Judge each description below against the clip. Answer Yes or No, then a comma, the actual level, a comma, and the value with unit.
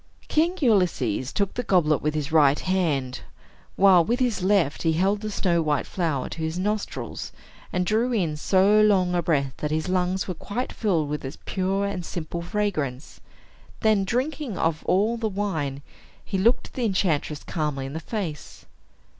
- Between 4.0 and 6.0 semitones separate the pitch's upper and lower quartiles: Yes, average, 5.1 semitones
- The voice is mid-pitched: Yes, medium, 180 Hz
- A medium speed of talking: Yes, average, 170 wpm